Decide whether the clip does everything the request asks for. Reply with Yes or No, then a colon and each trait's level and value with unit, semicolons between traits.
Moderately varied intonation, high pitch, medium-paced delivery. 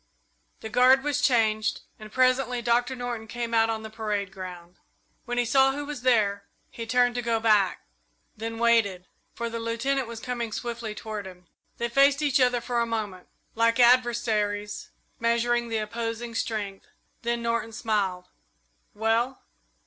No: narrow, 2.1 semitones; high, 230 Hz; average, 155 wpm